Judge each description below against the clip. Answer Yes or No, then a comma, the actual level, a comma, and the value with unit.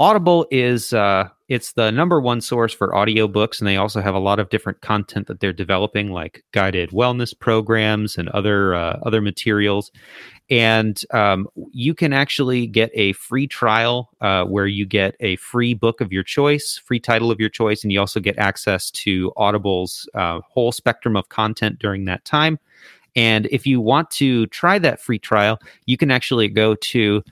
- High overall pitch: No, low, 110 Hz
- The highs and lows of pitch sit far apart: No, average, 3.3 semitones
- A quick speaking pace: No, average, 185 wpm